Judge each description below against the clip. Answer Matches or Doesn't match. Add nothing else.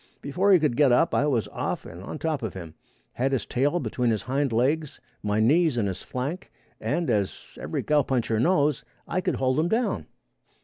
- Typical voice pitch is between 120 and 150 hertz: Matches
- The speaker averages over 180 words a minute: Matches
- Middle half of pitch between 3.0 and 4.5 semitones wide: Doesn't match